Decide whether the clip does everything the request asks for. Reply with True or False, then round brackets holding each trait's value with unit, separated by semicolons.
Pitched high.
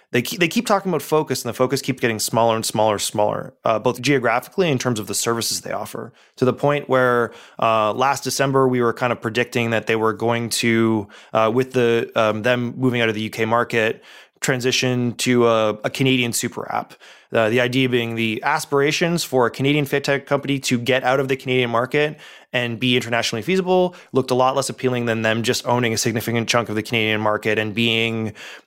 False (120 Hz)